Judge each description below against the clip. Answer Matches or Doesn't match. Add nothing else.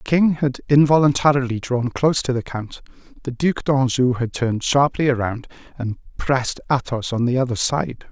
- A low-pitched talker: Matches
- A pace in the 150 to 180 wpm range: Matches